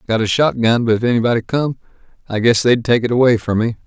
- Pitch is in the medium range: No, low, 115 Hz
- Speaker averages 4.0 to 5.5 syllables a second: No, 6.4 syllables/s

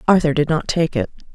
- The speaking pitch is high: No, medium, 165 Hz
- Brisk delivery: Yes, fast, 225 wpm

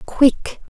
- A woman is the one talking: Yes, female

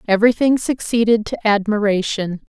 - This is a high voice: Yes, high, 215 Hz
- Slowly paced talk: Yes, slow, 95 wpm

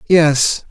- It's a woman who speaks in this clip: No, male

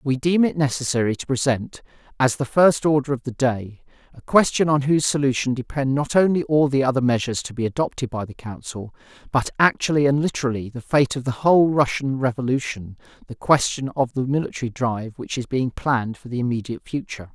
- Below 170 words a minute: No, average, 195 wpm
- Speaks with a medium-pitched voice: No, low, 130 Hz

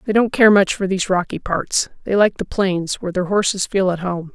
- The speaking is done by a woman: Yes, female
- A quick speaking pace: Yes, fast, 250 wpm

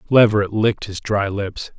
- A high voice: No, low, 105 Hz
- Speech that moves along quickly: No, average, 170 wpm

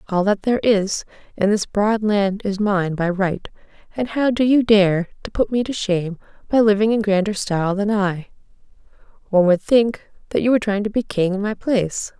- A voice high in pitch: Yes, high, 205 Hz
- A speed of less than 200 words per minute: No, fast, 205 wpm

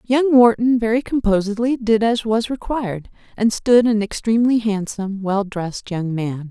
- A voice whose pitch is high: Yes, high, 220 Hz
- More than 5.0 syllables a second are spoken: No, 4.9 syllables/s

